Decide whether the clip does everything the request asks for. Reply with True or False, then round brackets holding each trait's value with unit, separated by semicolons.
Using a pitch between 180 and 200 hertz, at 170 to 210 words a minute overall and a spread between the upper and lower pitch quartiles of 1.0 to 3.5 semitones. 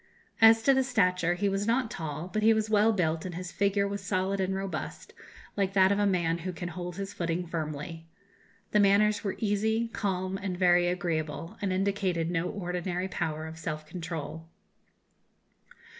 True (185 Hz; 175 wpm; 3.1 semitones)